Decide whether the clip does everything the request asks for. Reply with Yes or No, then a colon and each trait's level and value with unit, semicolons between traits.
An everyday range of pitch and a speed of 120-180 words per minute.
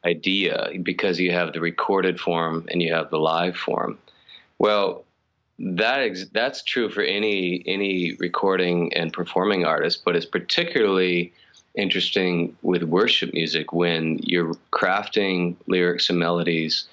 No: narrow, 1.3 semitones; slow, 135 wpm